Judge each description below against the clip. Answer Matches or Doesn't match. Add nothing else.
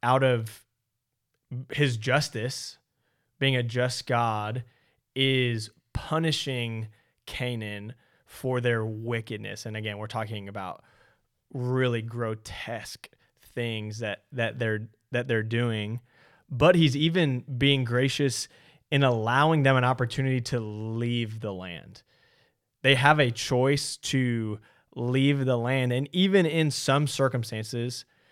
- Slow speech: Matches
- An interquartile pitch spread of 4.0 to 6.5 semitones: Doesn't match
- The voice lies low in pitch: Matches